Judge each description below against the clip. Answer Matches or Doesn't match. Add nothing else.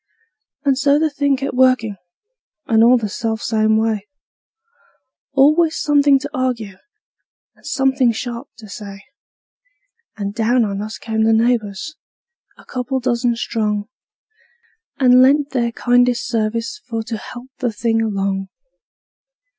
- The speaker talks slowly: Matches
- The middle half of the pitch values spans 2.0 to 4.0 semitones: Matches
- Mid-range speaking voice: Doesn't match